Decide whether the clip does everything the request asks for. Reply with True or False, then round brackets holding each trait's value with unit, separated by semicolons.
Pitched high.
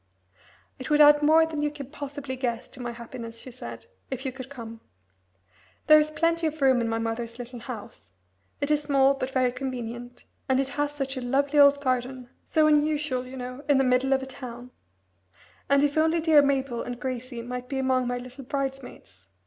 True (265 Hz)